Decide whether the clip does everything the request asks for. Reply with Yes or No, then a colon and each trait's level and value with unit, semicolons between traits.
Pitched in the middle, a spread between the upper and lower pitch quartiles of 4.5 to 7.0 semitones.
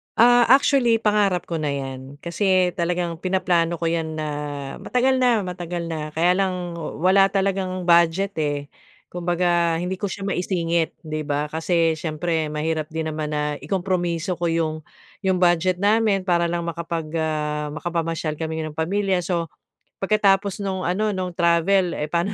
No: medium, 170 Hz; average, 2.9 semitones